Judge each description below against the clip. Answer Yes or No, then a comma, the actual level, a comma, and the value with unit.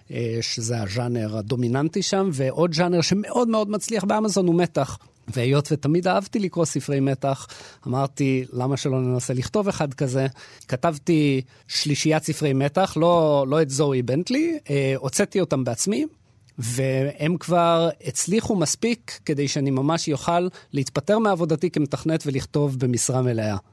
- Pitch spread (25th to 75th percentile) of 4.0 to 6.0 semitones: Yes, average, 4.7 semitones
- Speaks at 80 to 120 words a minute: No, average, 130 wpm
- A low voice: No, medium, 145 Hz